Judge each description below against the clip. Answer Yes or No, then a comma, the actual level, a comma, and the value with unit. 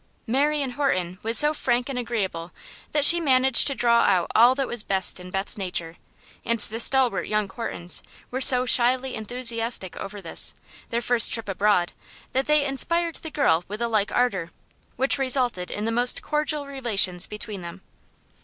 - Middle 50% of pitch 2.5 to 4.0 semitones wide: No, average, 5.1 semitones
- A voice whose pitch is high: Yes, high, 235 Hz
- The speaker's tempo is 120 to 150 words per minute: No, average, 175 wpm